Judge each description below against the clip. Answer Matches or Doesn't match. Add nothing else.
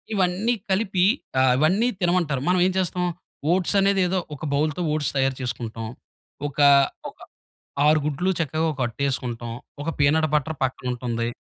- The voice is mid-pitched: Matches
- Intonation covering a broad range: Matches